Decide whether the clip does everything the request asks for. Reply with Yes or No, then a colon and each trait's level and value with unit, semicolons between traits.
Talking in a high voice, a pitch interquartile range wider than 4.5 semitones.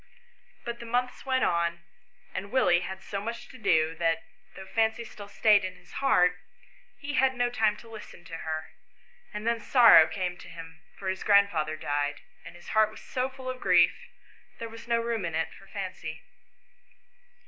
Yes: high, 200 Hz; average, 5.2 semitones